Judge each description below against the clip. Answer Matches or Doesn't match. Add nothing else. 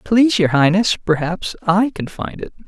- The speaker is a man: Matches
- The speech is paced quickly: Doesn't match